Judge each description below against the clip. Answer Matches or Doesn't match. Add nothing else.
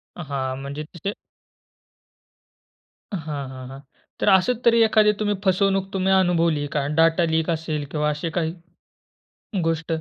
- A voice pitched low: Doesn't match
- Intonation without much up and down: Doesn't match